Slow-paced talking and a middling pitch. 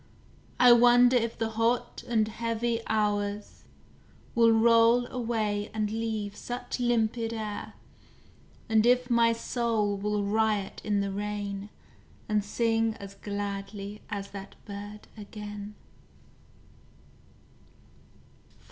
No: slow, 105 wpm; high, 220 Hz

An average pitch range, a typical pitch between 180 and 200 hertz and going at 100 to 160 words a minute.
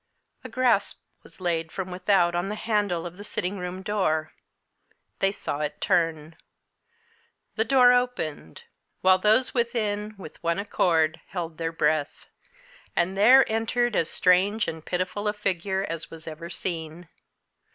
Yes: average, 4.1 semitones; medium, 185 Hz; average, 145 wpm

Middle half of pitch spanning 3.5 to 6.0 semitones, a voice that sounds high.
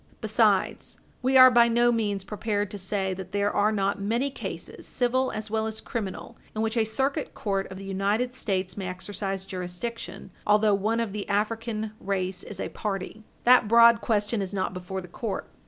No: average, 2.9 semitones; high, 210 Hz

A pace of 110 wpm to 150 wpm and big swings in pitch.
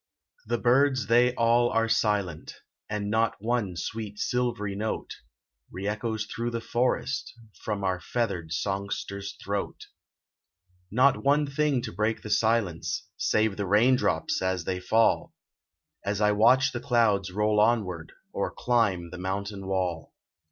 No: average, 140 wpm; average, 3.3 semitones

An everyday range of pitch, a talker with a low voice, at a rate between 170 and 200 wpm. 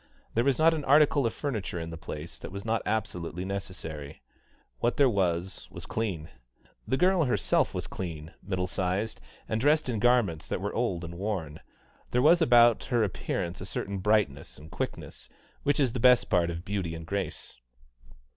No: wide, 6.2 semitones; low, 100 Hz; average, 180 wpm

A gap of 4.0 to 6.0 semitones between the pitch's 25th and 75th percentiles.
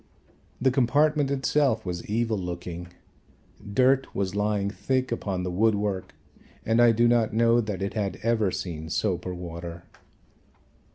Yes: average, 4.5 semitones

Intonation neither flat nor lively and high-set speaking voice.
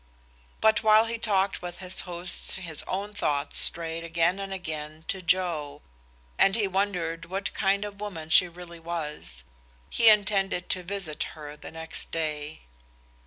No: average, 3.4 semitones; medium, 180 Hz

